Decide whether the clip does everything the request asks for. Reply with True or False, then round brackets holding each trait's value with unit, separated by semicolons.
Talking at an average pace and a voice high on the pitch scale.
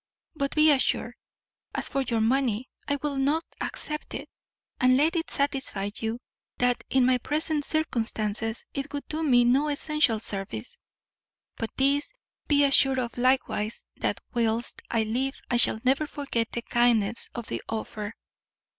True (155 wpm; 255 Hz)